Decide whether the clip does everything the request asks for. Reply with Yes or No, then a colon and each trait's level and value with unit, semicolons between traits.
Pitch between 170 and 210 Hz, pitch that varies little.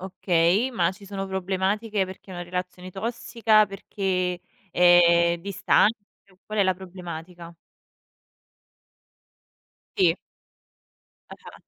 Yes: medium, 185 Hz; narrow, 2.2 semitones